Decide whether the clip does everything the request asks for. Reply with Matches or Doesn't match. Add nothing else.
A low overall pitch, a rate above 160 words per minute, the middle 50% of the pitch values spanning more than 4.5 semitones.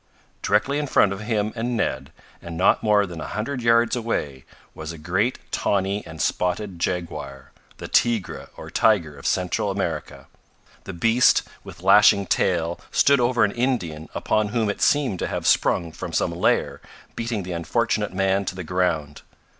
Matches